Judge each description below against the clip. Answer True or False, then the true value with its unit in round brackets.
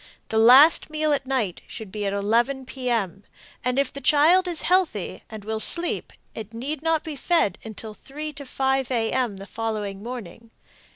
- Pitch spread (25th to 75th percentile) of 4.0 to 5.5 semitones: True (5.0 semitones)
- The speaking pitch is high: True (250 Hz)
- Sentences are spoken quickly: False (185 wpm)